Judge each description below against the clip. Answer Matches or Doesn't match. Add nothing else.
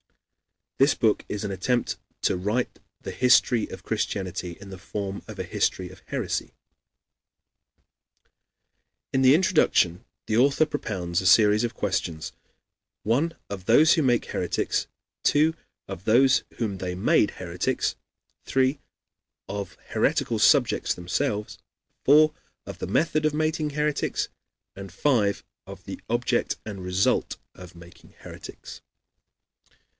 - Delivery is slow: Matches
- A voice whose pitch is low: Matches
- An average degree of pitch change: Doesn't match